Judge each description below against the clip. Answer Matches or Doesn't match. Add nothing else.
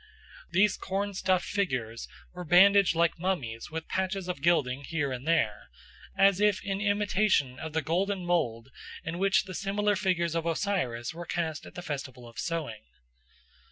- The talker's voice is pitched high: Doesn't match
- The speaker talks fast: Doesn't match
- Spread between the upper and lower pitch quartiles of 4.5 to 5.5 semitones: Matches